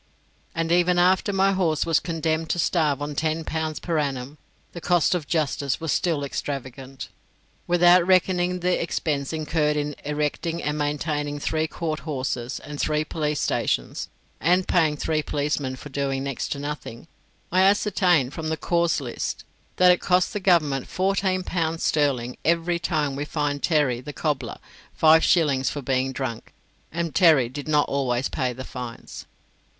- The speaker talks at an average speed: Yes, average, 160 wpm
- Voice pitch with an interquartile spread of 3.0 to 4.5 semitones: Yes, average, 3.4 semitones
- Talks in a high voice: No, medium, 155 Hz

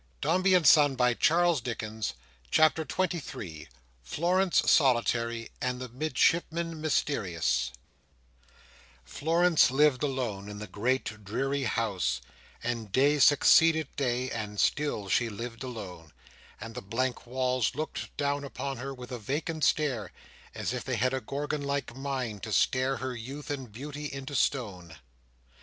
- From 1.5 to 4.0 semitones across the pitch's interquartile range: No, average, 4.5 semitones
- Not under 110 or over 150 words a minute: Yes, average, 145 wpm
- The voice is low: Yes, low, 130 Hz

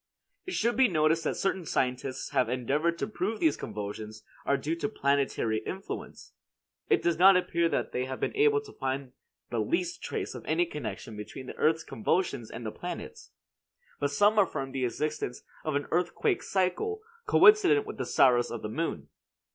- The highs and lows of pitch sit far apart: Yes, wide, 7.2 semitones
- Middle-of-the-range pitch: Yes, medium, 155 Hz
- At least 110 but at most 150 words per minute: No, average, 180 wpm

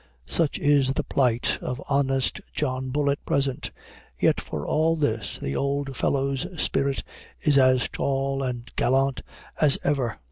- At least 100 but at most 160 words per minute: Yes, average, 150 wpm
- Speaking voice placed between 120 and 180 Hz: Yes, low, 135 Hz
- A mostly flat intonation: Yes, narrow, 1.7 semitones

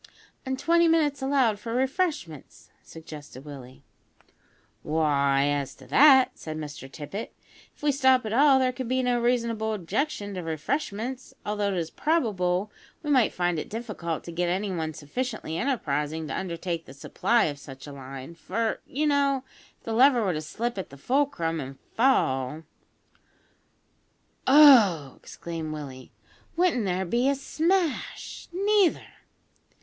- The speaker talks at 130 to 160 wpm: Yes, average, 150 wpm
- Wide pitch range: Yes, wide, 9.0 semitones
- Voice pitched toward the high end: Yes, high, 210 Hz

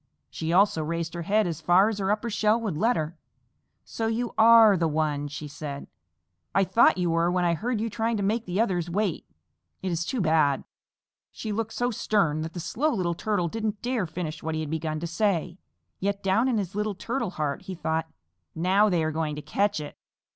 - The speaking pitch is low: No, medium, 185 Hz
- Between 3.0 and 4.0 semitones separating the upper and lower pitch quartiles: No, average, 5.0 semitones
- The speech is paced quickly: Yes, fast, 215 wpm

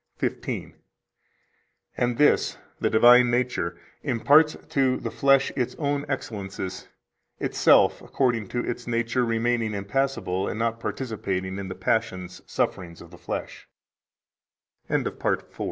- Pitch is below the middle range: Yes, low, 115 Hz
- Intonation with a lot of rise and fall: No, average, 4.4 semitones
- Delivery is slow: Yes, slow, 105 wpm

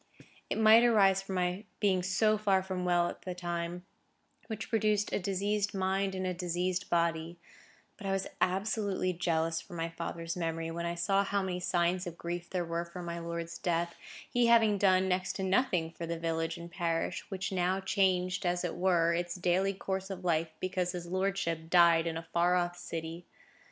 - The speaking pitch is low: No, medium, 180 Hz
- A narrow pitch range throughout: Yes, narrow, 2.2 semitones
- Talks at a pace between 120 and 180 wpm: No, average, 190 wpm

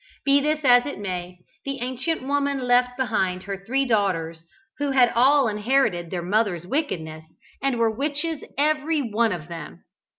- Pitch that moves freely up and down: Yes, wide, 6.9 semitones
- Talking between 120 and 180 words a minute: Yes, average, 160 wpm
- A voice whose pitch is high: Yes, high, 245 Hz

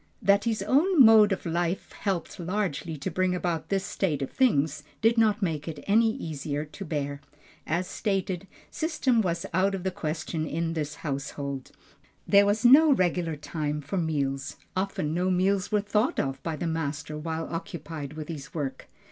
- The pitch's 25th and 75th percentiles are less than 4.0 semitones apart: No, average, 4.8 semitones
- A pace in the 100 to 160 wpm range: No, average, 175 wpm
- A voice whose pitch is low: No, medium, 170 Hz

